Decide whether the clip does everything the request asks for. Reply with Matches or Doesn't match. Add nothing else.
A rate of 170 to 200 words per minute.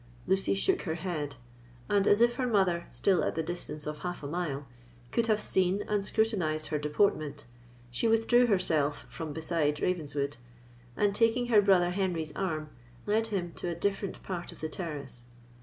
Matches